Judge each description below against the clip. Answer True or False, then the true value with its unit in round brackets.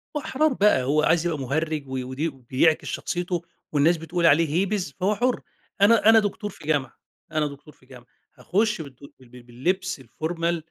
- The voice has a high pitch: False (160 Hz)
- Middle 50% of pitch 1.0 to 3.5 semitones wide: False (5.1 semitones)